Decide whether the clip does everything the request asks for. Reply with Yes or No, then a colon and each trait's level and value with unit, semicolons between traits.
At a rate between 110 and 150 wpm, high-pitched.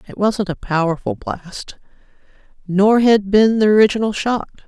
Yes: average, 140 wpm; high, 200 Hz